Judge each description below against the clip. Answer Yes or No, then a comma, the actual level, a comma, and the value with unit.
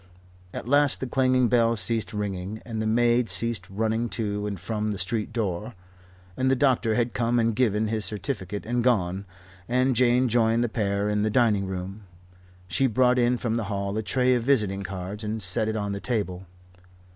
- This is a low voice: Yes, low, 110 Hz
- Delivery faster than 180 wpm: Yes, average, 190 wpm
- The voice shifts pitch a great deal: No, average, 3.0 semitones